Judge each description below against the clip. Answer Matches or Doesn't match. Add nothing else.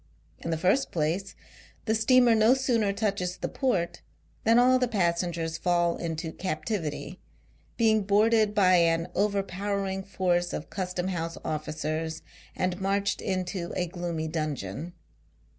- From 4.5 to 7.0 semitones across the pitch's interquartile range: Doesn't match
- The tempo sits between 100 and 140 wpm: Matches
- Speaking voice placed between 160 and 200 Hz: Matches